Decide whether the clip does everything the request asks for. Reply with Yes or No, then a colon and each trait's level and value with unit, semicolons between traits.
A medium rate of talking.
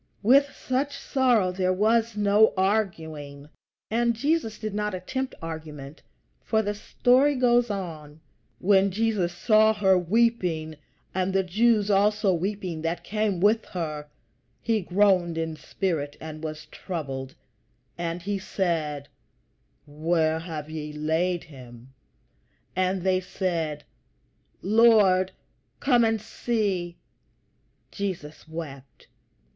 No: slow, 115 wpm